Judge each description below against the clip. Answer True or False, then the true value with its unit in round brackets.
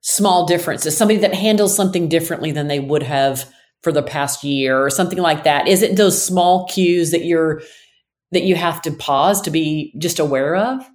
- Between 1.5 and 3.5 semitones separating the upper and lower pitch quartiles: False (3.9 semitones)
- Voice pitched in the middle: True (170 Hz)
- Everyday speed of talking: True (195 wpm)